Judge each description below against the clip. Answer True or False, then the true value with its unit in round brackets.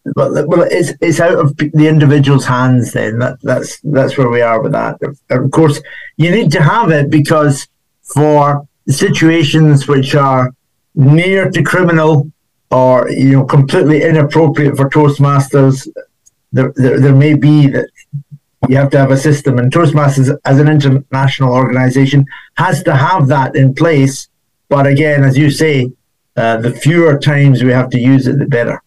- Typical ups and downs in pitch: False (2.3 semitones)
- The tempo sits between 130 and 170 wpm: True (165 wpm)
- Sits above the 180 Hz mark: False (140 Hz)